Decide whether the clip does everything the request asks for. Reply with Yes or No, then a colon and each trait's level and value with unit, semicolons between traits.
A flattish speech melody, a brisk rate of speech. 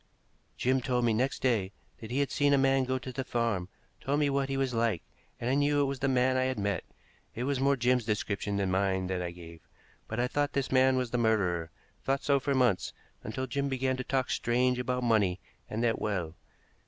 No: average, 4.0 semitones; fast, 230 wpm